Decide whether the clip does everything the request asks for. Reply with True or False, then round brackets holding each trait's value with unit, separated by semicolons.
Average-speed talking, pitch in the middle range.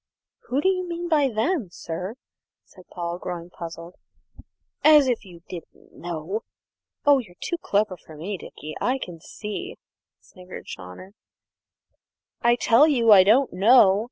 False (145 wpm; 205 Hz)